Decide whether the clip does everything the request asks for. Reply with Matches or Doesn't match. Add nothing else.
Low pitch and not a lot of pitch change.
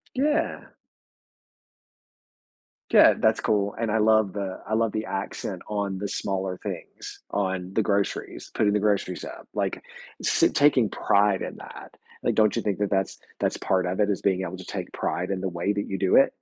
Matches